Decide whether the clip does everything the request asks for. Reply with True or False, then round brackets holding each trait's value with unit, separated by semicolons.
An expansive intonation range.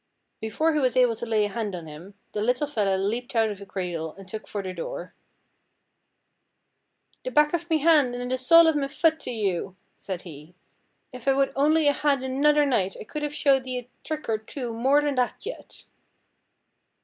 True (6.3 semitones)